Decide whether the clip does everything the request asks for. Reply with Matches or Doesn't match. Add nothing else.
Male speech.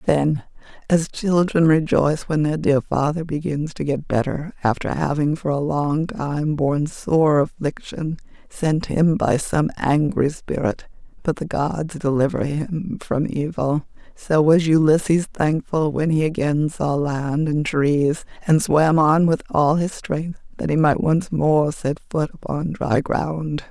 Doesn't match